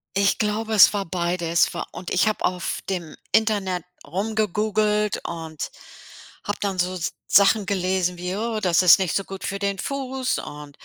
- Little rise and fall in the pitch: No, average, 3.0 semitones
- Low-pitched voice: No, high, 195 Hz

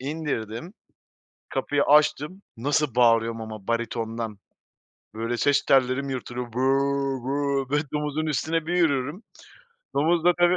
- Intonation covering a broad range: No, average, 4.5 semitones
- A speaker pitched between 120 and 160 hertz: Yes, medium, 140 Hz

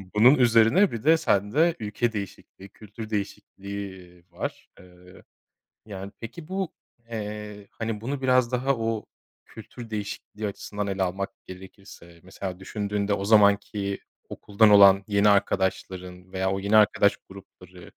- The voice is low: Yes, low, 100 Hz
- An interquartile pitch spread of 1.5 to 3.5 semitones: Yes, narrow, 2.6 semitones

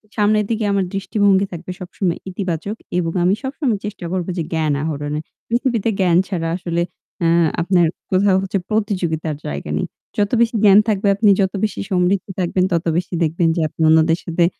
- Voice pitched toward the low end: No, medium, 185 Hz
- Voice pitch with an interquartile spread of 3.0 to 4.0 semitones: Yes, average, 3.5 semitones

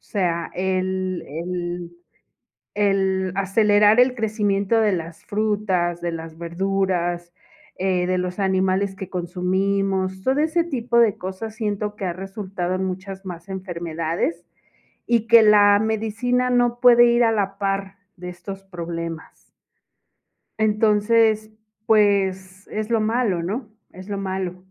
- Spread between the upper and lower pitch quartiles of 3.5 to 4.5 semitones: No, average, 2.8 semitones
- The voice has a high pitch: Yes, high, 195 Hz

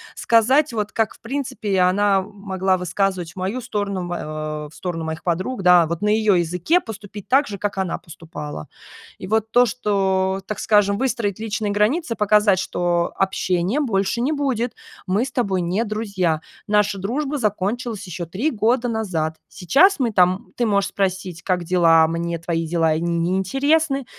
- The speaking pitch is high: Yes, high, 200 Hz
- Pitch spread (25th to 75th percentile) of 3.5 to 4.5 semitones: Yes, average, 4.1 semitones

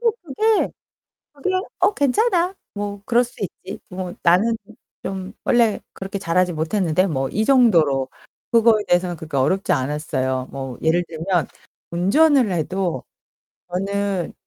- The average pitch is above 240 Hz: No, high, 190 Hz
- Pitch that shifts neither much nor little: No, wide, 6.1 semitones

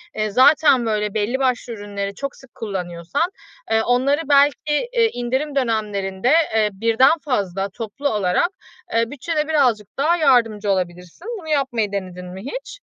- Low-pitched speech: No, high, 230 Hz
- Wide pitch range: Yes, wide, 5.8 semitones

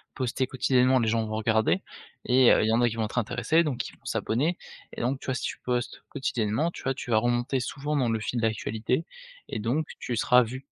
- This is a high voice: No, low, 125 Hz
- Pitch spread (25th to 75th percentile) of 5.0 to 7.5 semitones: No, average, 2.8 semitones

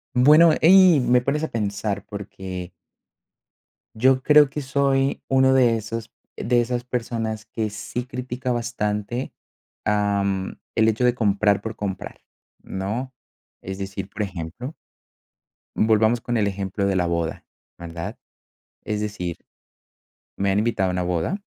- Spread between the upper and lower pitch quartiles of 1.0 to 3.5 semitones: No, average, 4.1 semitones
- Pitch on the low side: Yes, low, 110 Hz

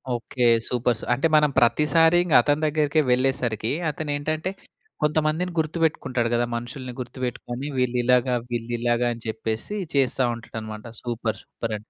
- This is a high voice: No, low, 125 Hz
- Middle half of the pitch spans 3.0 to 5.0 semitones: Yes, average, 4.2 semitones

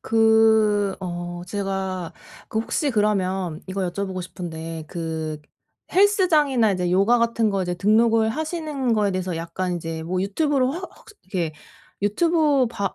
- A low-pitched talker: No, high, 200 Hz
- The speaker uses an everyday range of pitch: Yes, average, 4.6 semitones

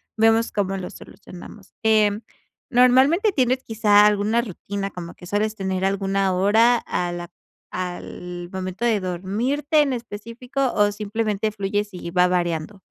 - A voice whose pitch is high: Yes, high, 205 Hz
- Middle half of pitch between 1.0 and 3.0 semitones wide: No, average, 3.7 semitones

